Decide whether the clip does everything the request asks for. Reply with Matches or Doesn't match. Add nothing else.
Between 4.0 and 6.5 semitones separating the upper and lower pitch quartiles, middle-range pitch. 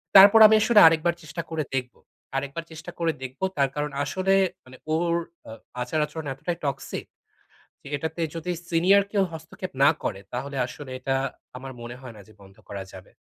Matches